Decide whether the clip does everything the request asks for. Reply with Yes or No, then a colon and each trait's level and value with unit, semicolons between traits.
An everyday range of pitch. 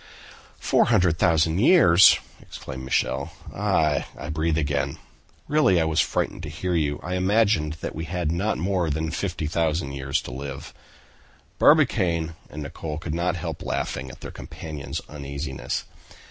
Yes: average, 3.3 semitones